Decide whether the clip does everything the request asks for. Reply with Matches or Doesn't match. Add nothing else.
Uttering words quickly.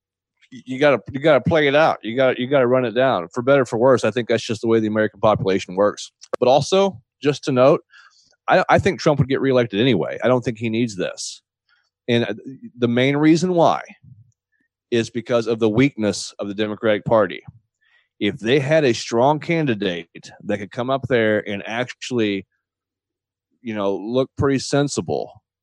Doesn't match